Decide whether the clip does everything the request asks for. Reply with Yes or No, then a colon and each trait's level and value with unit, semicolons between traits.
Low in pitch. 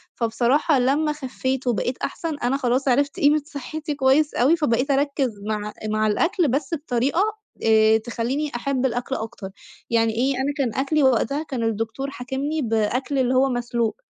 No: very high, 265 Hz